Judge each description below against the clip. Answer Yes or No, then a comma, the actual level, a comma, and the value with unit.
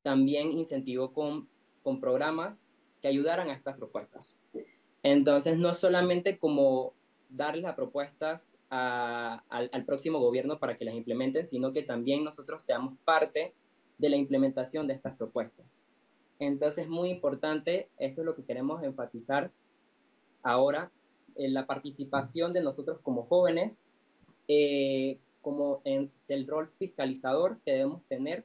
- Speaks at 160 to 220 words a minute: No, average, 135 wpm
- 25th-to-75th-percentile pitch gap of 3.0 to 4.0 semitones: Yes, average, 3.7 semitones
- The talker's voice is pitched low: No, medium, 145 Hz